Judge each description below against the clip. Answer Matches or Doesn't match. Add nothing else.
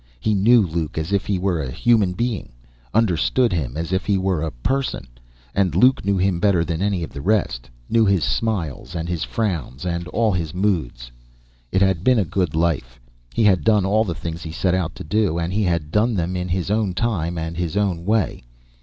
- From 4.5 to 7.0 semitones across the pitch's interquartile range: Doesn't match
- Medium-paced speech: Doesn't match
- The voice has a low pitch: Matches